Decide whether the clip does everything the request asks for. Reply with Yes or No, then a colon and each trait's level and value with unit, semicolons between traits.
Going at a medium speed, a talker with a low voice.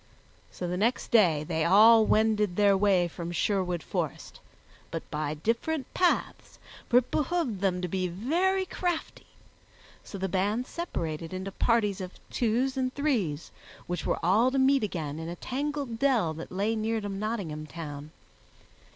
No: average, 160 wpm; high, 205 Hz